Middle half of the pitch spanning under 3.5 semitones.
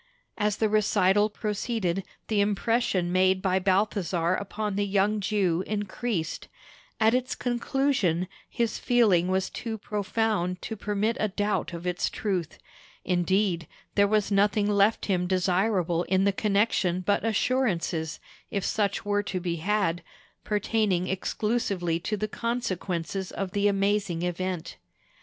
Yes: average, 2.7 semitones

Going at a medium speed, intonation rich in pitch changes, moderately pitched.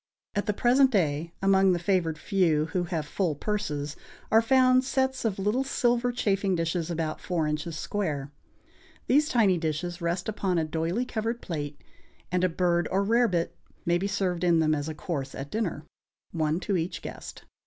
No: average, 175 wpm; average, 4.5 semitones; medium, 180 Hz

